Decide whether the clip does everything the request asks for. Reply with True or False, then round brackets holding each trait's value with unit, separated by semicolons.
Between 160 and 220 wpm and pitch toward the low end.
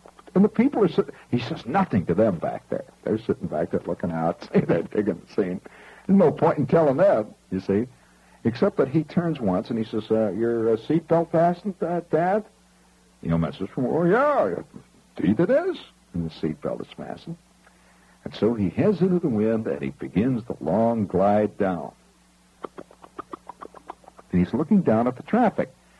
True (185 wpm; 115 Hz)